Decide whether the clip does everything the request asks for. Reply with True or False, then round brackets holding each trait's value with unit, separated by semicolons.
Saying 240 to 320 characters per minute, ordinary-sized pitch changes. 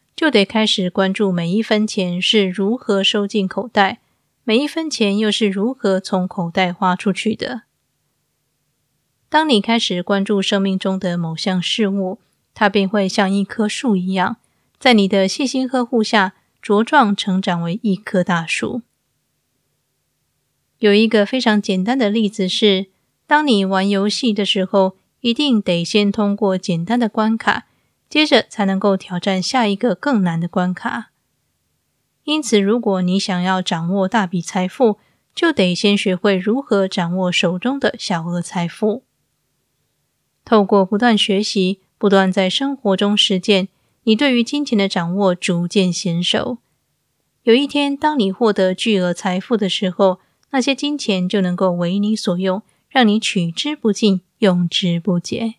False (225 characters per minute; 3.0 semitones)